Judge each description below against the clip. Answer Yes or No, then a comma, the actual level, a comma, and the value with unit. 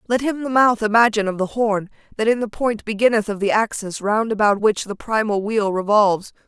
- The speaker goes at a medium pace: No, fast, 215 wpm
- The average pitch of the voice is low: No, high, 215 Hz